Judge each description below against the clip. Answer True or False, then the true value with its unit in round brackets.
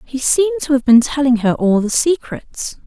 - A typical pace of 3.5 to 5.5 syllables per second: True (4.4 syllables/s)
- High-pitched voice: True (270 Hz)